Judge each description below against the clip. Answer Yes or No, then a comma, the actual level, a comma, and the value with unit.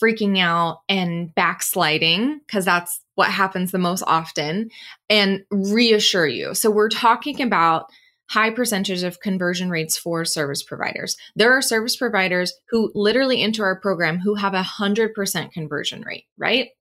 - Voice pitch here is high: Yes, high, 195 Hz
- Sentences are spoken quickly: No, average, 150 wpm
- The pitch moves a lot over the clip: No, average, 4.0 semitones